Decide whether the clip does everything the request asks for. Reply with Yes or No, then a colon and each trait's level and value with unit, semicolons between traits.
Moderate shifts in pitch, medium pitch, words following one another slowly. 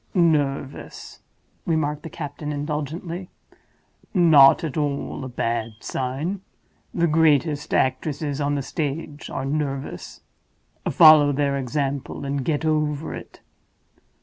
No: narrow, 2.3 semitones; medium, 145 Hz; slow, 110 wpm